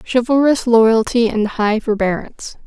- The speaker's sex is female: Yes, female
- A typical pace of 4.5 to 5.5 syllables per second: Yes, 4.7 syllables/s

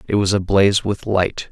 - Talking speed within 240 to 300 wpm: No, average, 200 wpm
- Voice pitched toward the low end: Yes, low, 100 Hz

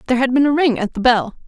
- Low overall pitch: No, very high, 250 Hz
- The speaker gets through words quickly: Yes, fast, 325 wpm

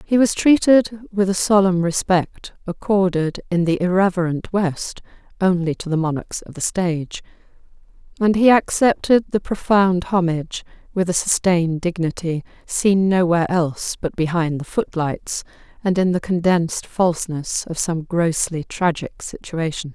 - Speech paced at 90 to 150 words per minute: Yes, average, 140 wpm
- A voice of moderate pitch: Yes, medium, 180 Hz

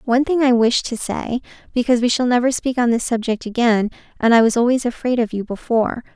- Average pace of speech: No, fast, 225 wpm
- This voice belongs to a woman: Yes, female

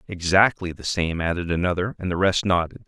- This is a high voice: No, very low, 90 Hz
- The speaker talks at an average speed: Yes, average, 190 wpm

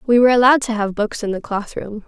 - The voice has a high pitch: Yes, high, 225 Hz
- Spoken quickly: Yes, fast, 290 wpm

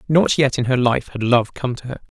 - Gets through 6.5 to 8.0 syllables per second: No, 5.3 syllables/s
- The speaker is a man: Yes, male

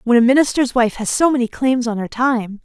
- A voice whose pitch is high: Yes, high, 240 Hz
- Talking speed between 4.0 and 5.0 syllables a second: No, 5.5 syllables/s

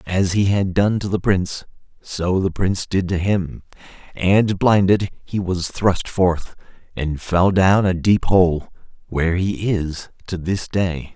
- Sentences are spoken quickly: No, average, 165 wpm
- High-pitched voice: No, very low, 95 Hz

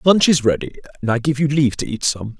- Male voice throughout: Yes, male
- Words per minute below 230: No, fast, 275 wpm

